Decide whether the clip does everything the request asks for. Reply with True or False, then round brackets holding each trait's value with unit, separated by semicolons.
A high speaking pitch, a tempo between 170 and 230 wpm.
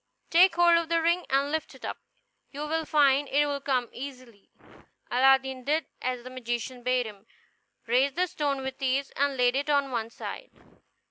True (270 Hz; 185 wpm)